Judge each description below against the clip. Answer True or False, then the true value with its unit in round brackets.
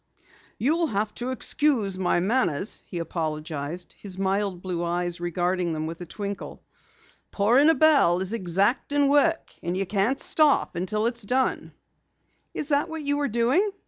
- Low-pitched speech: False (200 Hz)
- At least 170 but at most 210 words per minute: False (155 wpm)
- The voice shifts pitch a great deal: True (7.3 semitones)